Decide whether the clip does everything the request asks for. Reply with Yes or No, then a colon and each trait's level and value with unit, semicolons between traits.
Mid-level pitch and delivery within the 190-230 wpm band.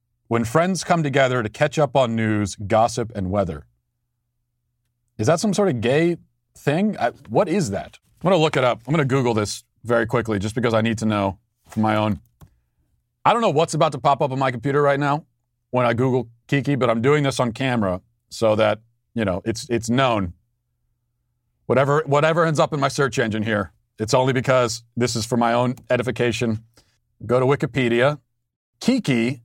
No: low, 120 Hz; average, 200 wpm